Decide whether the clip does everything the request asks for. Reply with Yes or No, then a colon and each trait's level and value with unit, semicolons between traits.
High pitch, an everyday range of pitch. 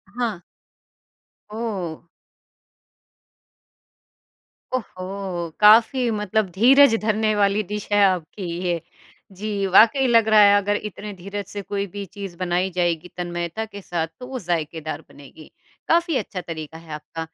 Yes: high, 200 Hz; average, 3.7 semitones